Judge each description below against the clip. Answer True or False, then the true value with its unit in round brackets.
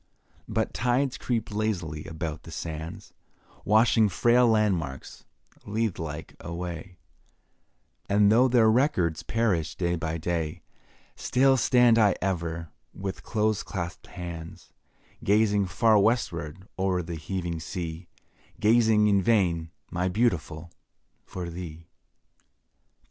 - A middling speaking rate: False (110 wpm)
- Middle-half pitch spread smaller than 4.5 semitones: False (4.8 semitones)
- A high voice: False (95 Hz)